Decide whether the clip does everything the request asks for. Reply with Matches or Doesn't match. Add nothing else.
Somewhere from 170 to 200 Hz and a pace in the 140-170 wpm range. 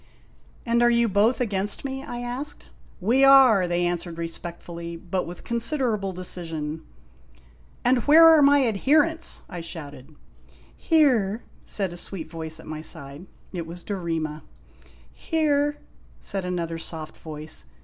Matches